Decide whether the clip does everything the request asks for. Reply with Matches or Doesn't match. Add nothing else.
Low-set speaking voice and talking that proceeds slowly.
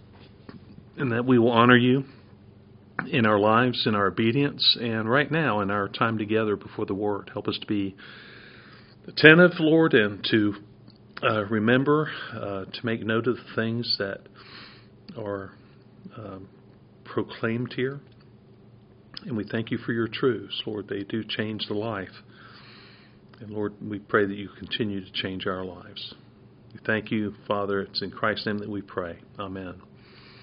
Doesn't match